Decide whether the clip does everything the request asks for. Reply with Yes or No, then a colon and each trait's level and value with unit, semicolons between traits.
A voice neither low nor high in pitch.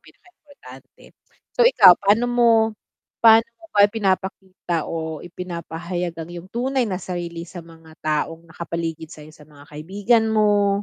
Yes: medium, 180 Hz